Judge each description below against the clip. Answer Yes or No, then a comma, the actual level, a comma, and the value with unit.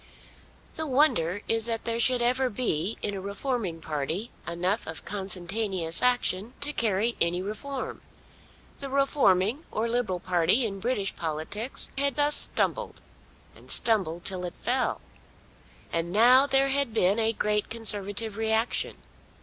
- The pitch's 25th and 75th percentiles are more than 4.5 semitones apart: Yes, average, 5.2 semitones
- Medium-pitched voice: No, high, 220 Hz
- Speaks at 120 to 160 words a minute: Yes, average, 140 wpm